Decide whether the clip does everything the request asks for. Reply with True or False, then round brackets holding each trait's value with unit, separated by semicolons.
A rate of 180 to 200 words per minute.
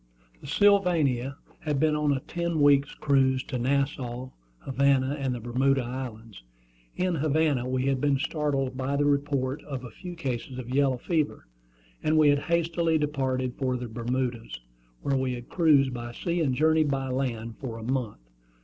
False (170 wpm)